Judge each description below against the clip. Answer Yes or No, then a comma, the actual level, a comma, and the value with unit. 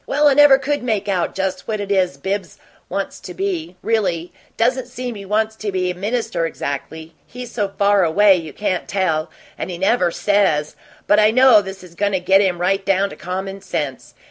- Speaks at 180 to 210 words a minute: Yes, fast, 205 wpm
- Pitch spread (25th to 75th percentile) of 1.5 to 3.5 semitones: Yes, average, 3.0 semitones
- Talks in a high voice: Yes, high, 195 Hz